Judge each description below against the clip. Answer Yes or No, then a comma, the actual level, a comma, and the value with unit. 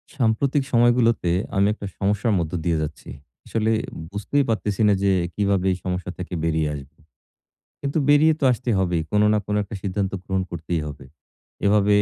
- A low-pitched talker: Yes, low, 100 Hz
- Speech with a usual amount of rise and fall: Yes, average, 4.0 semitones